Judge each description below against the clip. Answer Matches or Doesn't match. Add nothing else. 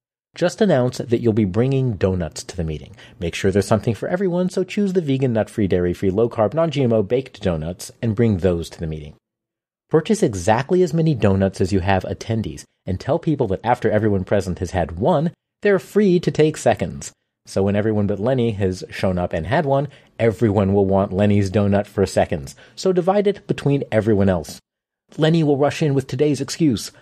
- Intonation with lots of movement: Matches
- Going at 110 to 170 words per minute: Doesn't match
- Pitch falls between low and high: Doesn't match